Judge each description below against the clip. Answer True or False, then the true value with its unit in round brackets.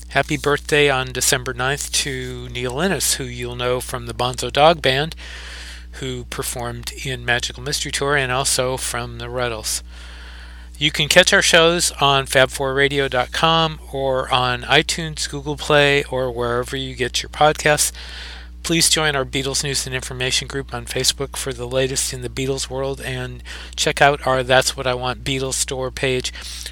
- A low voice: True (130 Hz)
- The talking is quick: False (165 wpm)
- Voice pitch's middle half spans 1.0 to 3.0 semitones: True (2.5 semitones)